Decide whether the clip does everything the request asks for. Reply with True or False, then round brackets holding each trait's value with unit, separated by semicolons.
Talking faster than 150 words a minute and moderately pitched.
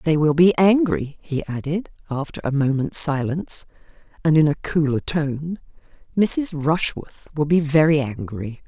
False (145 wpm; 155 Hz)